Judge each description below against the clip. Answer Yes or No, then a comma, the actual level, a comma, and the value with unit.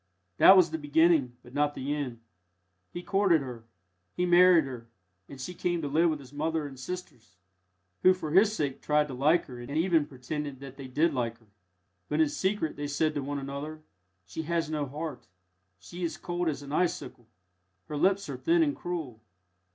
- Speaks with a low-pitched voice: No, medium, 150 Hz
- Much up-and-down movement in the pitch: No, average, 4.0 semitones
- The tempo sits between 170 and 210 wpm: Yes, average, 195 wpm